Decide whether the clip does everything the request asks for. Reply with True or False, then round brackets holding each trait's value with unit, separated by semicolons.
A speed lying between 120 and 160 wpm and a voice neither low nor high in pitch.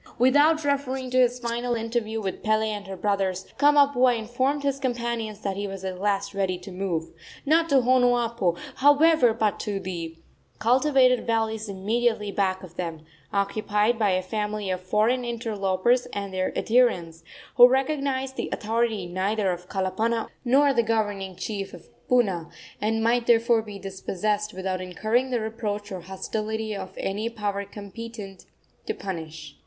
False (155 wpm; 215 Hz)